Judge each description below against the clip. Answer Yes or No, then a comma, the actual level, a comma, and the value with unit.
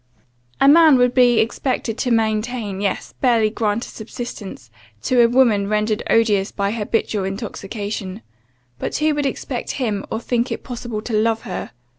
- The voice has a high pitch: Yes, high, 225 Hz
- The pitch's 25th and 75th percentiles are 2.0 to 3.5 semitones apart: Yes, average, 2.9 semitones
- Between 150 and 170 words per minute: Yes, average, 165 wpm